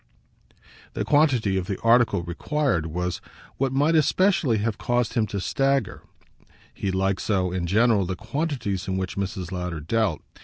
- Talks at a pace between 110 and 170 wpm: Yes, average, 155 wpm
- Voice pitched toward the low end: Yes, low, 100 Hz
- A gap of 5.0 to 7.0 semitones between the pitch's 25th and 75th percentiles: Yes, wide, 5.6 semitones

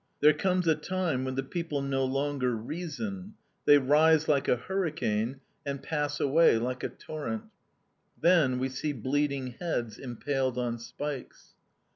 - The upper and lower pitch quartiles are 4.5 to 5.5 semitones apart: No, average, 3.7 semitones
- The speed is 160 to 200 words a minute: No, average, 145 wpm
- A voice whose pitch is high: No, medium, 145 Hz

